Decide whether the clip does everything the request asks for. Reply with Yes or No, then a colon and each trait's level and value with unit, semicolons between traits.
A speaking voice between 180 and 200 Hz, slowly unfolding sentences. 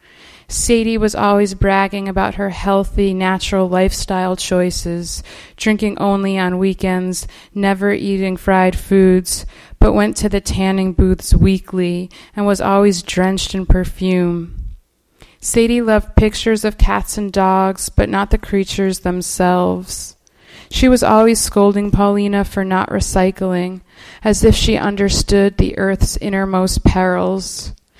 Yes: high, 190 Hz; slow, 125 wpm